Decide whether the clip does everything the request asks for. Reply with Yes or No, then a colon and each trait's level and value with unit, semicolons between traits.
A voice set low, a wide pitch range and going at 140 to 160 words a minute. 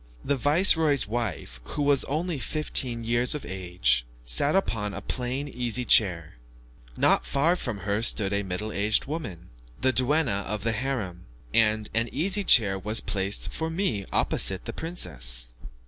Yes: low, 115 Hz; wide, 6.5 semitones; average, 155 wpm